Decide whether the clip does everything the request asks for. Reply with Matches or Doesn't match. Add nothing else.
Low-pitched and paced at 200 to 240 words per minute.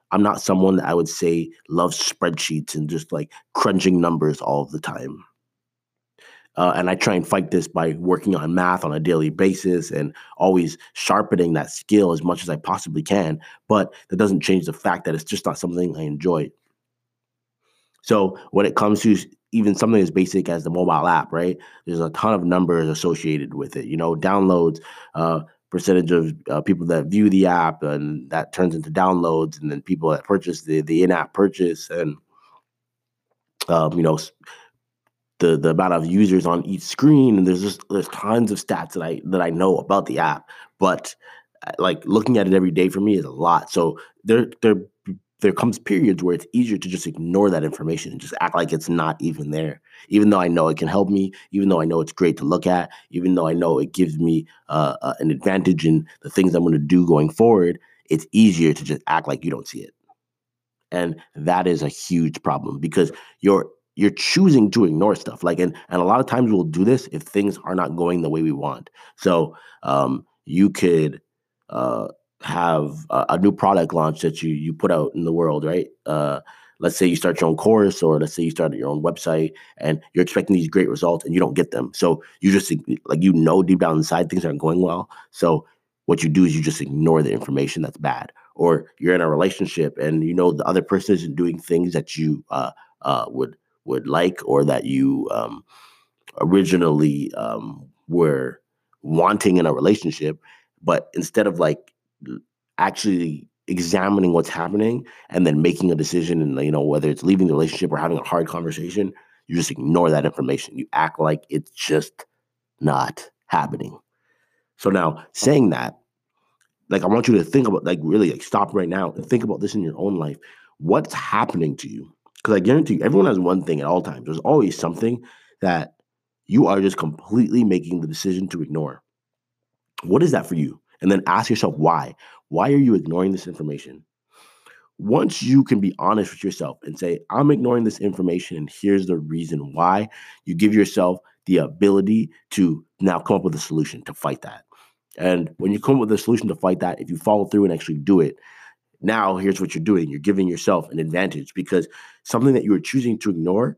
Matches